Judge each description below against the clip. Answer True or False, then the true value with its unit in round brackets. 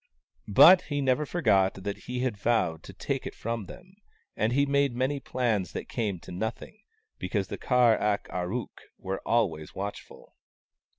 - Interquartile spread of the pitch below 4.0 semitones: False (5.0 semitones)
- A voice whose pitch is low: True (115 Hz)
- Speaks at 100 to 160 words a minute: False (170 wpm)